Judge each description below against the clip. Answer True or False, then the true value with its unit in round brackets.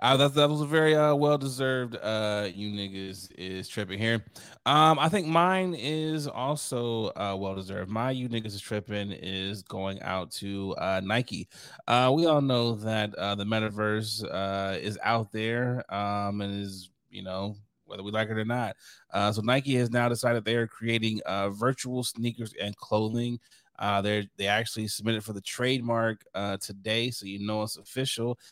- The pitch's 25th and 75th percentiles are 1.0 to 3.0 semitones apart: False (3.7 semitones)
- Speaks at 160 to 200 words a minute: True (180 wpm)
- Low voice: True (110 Hz)